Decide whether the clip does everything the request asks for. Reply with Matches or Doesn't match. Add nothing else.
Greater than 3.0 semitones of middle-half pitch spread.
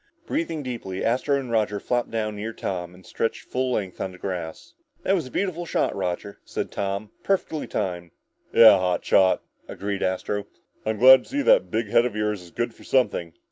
Matches